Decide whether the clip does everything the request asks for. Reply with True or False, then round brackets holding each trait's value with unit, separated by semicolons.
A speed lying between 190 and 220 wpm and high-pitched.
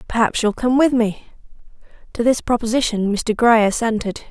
False (155 wpm; 230 Hz)